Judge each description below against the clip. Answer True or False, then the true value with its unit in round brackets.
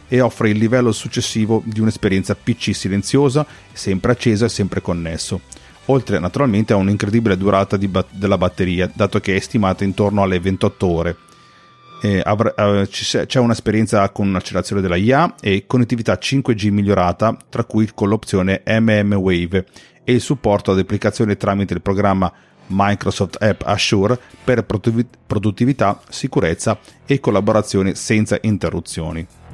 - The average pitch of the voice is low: True (105 Hz)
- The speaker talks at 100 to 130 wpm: False (140 wpm)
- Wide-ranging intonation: False (2.9 semitones)